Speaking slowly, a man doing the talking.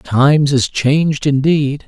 Yes: slow, 130 wpm; male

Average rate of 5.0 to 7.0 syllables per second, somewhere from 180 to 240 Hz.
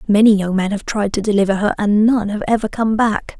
Yes: 5.7 syllables/s; high, 210 Hz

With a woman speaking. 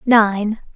Yes: female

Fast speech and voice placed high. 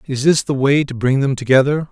No: fast, 250 wpm; low, 135 Hz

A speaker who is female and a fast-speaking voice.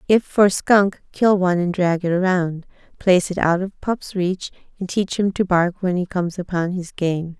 Yes: female; fast, 210 wpm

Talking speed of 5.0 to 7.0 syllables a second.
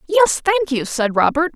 No: 4.5 syllables/s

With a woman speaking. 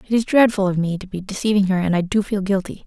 Yes: female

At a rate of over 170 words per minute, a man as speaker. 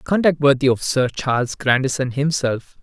No: average, 150 wpm; male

